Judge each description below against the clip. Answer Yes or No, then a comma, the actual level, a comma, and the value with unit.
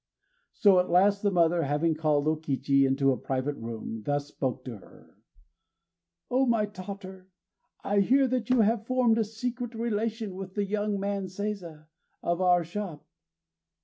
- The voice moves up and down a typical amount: No, wide, 5.7 semitones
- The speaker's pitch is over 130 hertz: Yes, high, 190 Hz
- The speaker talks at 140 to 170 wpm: Yes, average, 165 wpm